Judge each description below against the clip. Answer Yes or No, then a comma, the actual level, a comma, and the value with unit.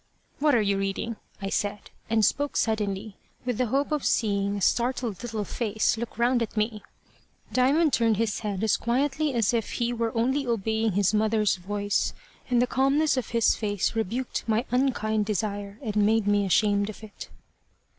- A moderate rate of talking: Yes, average, 175 wpm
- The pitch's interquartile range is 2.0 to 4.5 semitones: Yes, average, 2.9 semitones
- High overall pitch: Yes, high, 220 Hz